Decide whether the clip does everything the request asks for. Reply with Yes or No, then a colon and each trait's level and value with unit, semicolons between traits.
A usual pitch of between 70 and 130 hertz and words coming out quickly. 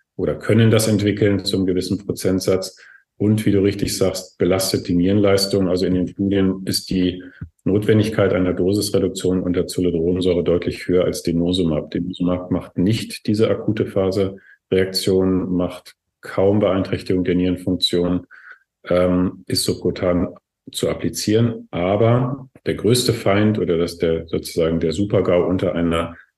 No: very low, 95 Hz; average, 135 wpm